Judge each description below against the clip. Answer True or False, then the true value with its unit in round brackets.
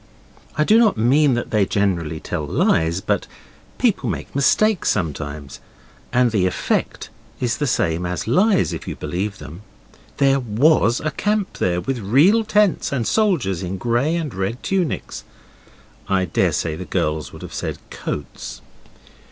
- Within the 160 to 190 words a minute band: False (150 wpm)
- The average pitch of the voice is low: True (120 Hz)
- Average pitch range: False (9.0 semitones)